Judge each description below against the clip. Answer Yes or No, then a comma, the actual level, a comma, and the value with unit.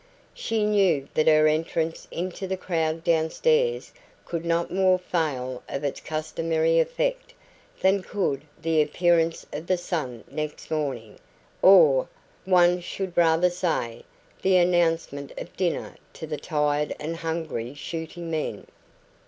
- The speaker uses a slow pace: Yes, slow, 130 wpm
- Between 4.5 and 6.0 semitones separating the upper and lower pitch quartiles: No, average, 2.8 semitones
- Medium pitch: Yes, medium, 165 Hz